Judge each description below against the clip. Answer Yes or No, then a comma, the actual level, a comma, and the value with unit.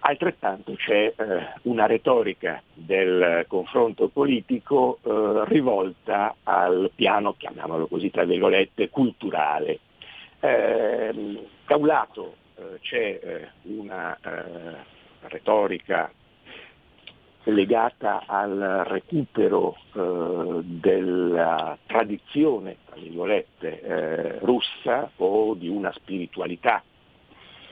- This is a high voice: Yes, very high, 255 Hz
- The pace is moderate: No, slow, 70 wpm